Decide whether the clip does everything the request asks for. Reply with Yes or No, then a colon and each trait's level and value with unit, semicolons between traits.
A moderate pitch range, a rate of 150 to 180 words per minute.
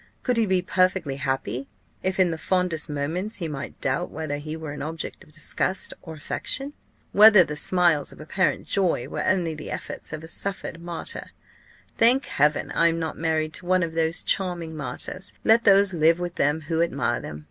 No: average, 3.2 semitones; average, 190 wpm